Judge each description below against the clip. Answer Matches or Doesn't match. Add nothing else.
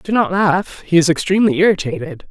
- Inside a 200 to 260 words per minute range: Doesn't match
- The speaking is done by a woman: Matches